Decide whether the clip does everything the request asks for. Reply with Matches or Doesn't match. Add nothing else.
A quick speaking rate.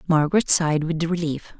Doesn't match